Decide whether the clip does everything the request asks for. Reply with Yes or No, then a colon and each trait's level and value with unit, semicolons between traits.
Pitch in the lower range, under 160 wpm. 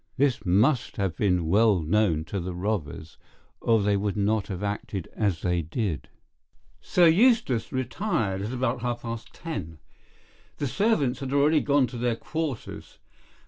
Yes: low, 110 Hz; average, 145 wpm